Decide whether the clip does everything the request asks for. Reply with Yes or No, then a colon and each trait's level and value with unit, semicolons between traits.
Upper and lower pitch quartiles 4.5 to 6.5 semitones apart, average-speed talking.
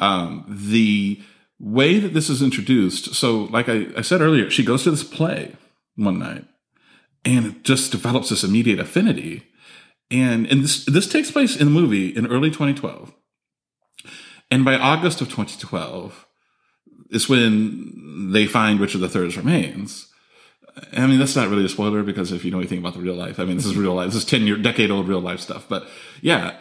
Yes: average, 5.2 semitones; average, 190 wpm